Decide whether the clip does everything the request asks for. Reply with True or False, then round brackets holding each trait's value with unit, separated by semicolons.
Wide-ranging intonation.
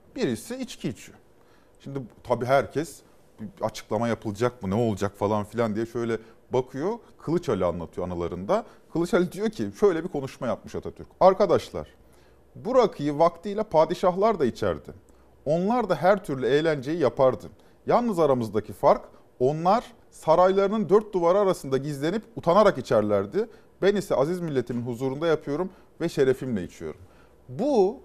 True (8.1 semitones)